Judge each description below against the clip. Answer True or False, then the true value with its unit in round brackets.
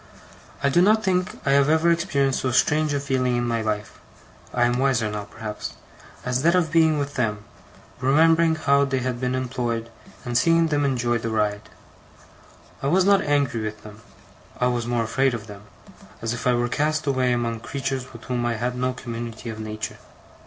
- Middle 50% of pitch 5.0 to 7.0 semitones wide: False (3.8 semitones)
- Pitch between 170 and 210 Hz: False (125 Hz)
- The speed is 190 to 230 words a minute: True (195 wpm)